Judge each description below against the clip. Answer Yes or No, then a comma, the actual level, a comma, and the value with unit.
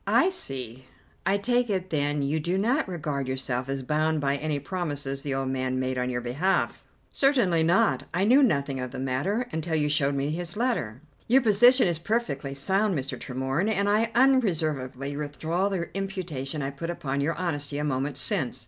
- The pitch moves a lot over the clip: Yes, wide, 6.1 semitones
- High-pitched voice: No, medium, 150 Hz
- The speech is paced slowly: No, average, 185 wpm